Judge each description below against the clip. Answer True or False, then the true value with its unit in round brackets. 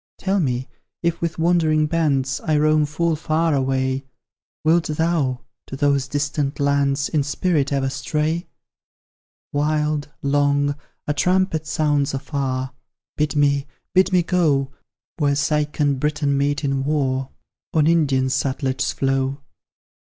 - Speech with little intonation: True (2.2 semitones)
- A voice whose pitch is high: False (145 Hz)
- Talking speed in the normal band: False (130 wpm)